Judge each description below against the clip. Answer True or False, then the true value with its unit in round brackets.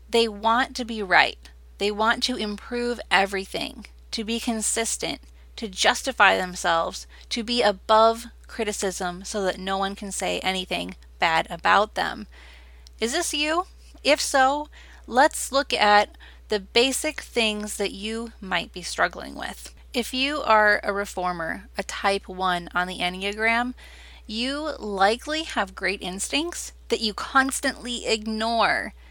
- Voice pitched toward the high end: True (215 Hz)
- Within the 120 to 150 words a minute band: True (140 wpm)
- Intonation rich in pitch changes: False (4.3 semitones)